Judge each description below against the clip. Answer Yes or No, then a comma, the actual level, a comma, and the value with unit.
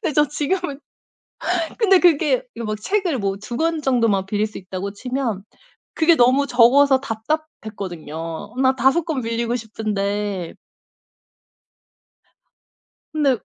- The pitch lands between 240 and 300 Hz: Yes, high, 245 Hz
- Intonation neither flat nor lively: No, wide, 6.0 semitones